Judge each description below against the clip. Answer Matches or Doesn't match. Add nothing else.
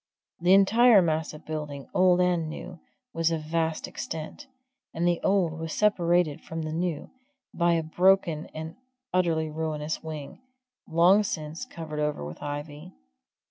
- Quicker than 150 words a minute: Doesn't match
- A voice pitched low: Doesn't match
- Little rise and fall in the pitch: Matches